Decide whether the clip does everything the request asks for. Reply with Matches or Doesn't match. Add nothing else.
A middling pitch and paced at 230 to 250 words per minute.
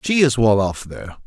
Doesn't match